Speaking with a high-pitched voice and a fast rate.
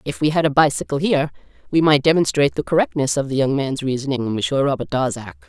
No: medium, 140 Hz; fast, 210 wpm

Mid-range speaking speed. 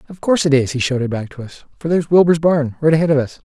No: fast, 275 wpm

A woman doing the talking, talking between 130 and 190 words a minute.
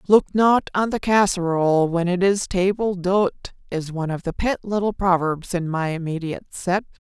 Yes: female; average, 180 wpm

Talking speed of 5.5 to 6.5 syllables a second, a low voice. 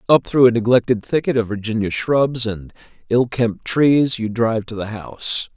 No: 4.8 syllables/s; low, 115 Hz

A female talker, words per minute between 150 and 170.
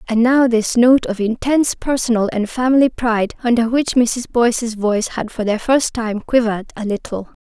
No: female; average, 185 wpm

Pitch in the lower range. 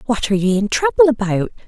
No: high, 230 Hz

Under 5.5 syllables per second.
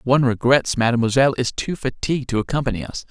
No: 6.7 syllables/s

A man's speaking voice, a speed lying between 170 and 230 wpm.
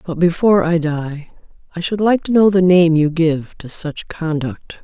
No: female; average, 200 wpm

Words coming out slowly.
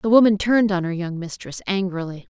No: fast, 205 wpm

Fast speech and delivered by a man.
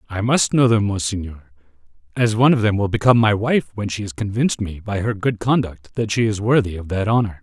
Yes: fast, 235 wpm; male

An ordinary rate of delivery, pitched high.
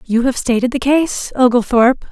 Yes: average, 170 wpm; high, 245 Hz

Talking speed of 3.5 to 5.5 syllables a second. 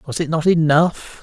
Yes: 4.2 syllables/s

